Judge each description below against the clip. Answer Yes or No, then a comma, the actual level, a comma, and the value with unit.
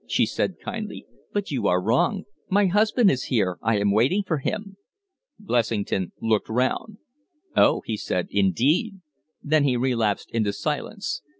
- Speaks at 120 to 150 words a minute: Yes, average, 145 wpm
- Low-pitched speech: Yes, low, 125 Hz